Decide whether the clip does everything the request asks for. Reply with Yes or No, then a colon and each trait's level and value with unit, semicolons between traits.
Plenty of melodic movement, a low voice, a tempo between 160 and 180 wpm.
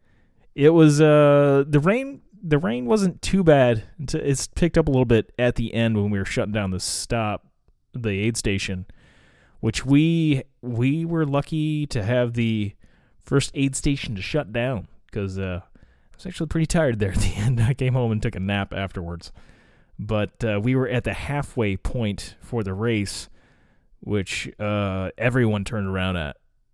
Yes: wide, 5.9 semitones; low, 120 Hz; average, 175 wpm